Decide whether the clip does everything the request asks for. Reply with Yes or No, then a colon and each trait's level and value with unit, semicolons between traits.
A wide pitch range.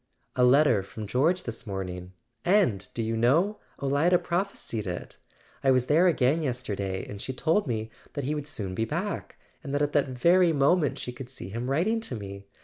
Yes: wide, 6.5 semitones